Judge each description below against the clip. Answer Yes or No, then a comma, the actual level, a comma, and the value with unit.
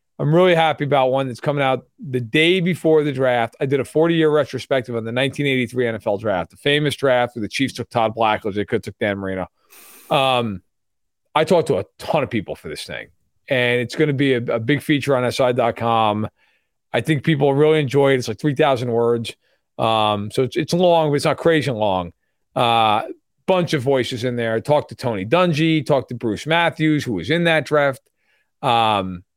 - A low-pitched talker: Yes, low, 130 Hz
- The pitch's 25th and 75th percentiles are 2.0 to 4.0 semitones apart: No, average, 4.8 semitones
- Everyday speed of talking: No, fast, 210 wpm